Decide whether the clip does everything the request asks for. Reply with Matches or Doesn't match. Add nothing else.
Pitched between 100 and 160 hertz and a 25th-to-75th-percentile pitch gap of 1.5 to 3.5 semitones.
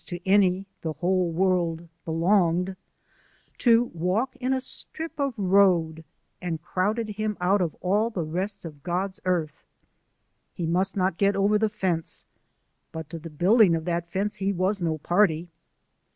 Doesn't match